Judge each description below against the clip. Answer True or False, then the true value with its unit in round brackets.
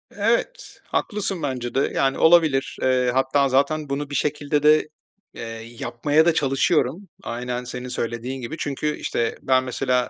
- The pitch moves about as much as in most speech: True (3.4 semitones)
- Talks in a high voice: False (140 Hz)